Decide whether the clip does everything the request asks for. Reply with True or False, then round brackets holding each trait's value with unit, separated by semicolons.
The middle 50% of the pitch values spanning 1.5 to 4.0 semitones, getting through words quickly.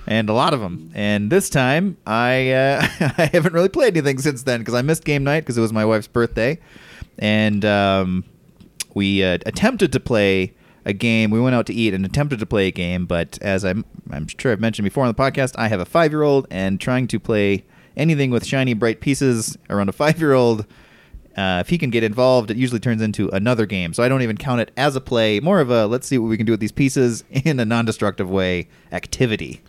False (4.5 semitones; 240 wpm)